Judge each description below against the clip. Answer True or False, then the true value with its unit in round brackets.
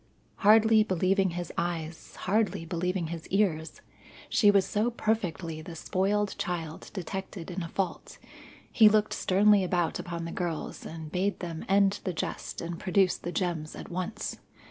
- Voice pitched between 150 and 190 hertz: True (185 Hz)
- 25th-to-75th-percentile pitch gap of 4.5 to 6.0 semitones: False (3.2 semitones)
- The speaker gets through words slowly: False (155 wpm)